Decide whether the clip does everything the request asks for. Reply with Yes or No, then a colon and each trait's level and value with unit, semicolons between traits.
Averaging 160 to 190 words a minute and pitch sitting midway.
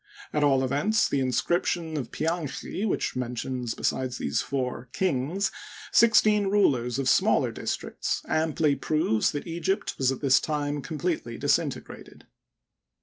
No: average, 140 wpm; medium, 145 Hz